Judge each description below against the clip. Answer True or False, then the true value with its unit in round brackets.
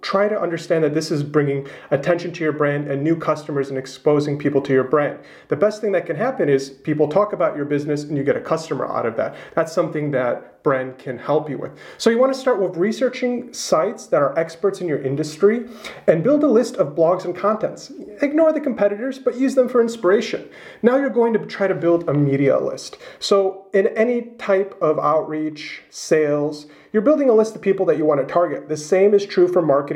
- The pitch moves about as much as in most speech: False (6.7 semitones)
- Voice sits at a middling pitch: True (175 Hz)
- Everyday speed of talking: False (225 wpm)